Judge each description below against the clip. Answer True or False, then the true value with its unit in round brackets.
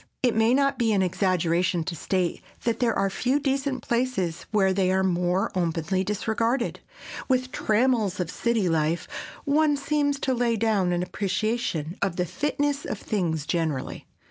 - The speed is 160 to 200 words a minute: True (165 wpm)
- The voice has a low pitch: False (205 Hz)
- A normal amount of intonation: False (5.7 semitones)